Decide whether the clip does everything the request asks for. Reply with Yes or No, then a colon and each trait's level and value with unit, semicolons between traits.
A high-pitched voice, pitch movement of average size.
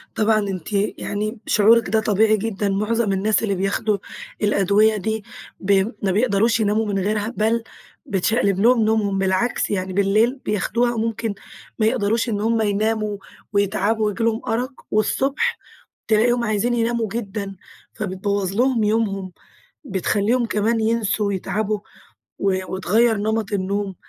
No: high, 215 Hz; narrow, 2.1 semitones